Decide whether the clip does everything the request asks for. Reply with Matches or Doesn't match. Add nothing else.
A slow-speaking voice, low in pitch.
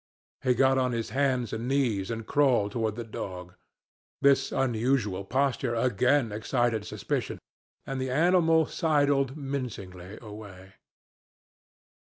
Matches